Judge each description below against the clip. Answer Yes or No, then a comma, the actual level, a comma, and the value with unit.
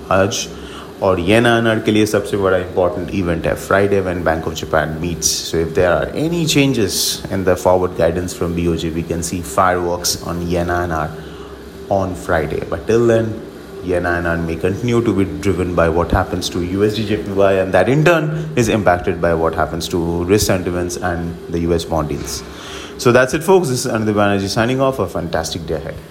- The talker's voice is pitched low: Yes, very low, 90 Hz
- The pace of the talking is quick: No, average, 185 wpm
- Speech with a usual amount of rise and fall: Yes, average, 3.8 semitones